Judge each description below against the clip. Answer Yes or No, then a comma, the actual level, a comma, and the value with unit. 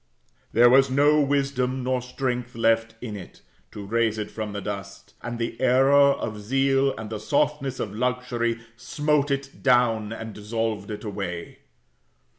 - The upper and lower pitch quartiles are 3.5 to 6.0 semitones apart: Yes, average, 3.8 semitones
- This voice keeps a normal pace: Yes, average, 155 wpm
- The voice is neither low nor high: No, low, 120 Hz